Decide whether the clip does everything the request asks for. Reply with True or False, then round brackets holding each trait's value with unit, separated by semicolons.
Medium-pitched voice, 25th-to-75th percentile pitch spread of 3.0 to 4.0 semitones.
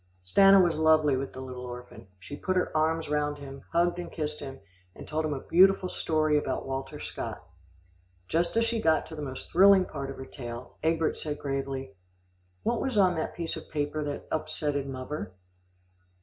True (150 Hz; 3.7 semitones)